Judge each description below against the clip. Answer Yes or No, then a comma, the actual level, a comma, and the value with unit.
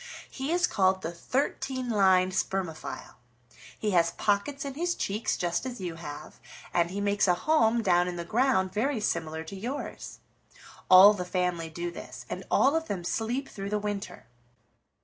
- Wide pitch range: Yes, wide, 5.7 semitones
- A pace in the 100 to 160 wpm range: No, average, 170 wpm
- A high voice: Yes, high, 200 Hz